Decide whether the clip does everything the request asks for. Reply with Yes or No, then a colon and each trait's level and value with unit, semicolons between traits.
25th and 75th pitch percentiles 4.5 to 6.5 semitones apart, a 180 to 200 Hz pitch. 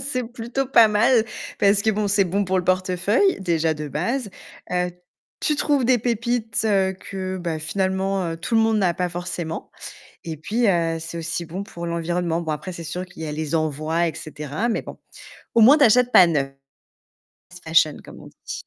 Yes: average, 5.1 semitones; medium, 185 Hz